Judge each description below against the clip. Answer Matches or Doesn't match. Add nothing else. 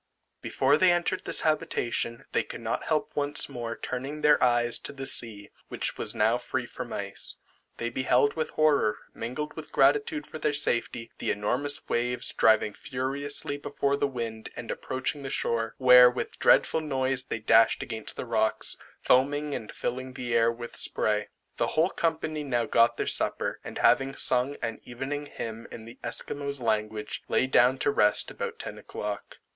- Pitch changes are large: Doesn't match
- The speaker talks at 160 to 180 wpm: Matches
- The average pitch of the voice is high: Doesn't match